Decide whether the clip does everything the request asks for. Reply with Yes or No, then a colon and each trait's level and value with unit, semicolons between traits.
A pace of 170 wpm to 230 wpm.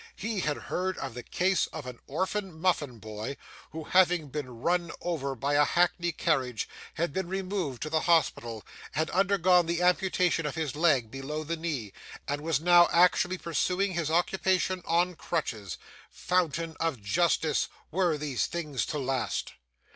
No: average, 160 wpm